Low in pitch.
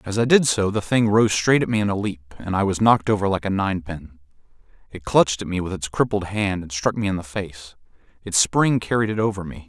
Yes: low, 100 Hz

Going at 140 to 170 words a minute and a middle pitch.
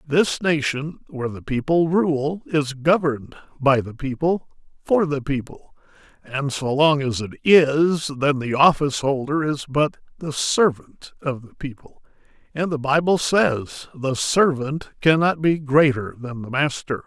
Yes: average, 145 wpm; medium, 145 Hz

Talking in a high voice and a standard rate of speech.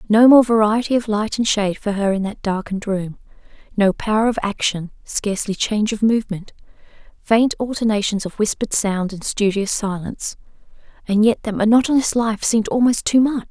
Yes: high, 215 Hz; average, 170 wpm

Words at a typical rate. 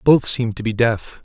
No: fast, 240 wpm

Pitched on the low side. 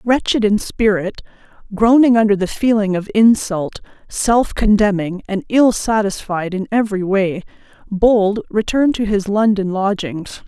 No: high, 205 Hz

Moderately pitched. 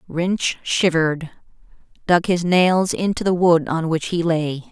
Yes: medium, 170 Hz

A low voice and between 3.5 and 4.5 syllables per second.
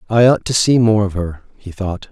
No: low, 100 Hz; 5.1 syllables/s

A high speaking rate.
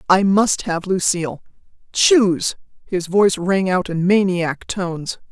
No: slow, 135 wpm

